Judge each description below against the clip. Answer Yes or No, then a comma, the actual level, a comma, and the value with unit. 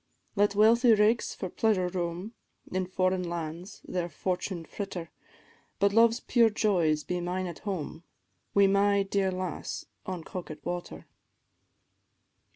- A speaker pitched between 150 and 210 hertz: Yes, medium, 185 Hz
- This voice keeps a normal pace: No, slow, 130 wpm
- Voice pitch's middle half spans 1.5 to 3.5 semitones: Yes, average, 2.7 semitones